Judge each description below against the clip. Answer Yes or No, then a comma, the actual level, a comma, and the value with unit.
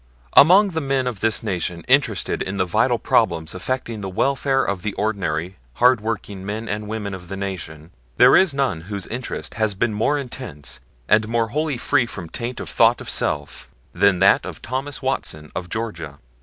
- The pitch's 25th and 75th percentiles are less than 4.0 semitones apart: No, wide, 5.5 semitones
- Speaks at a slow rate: No, average, 185 wpm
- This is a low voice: Yes, low, 105 Hz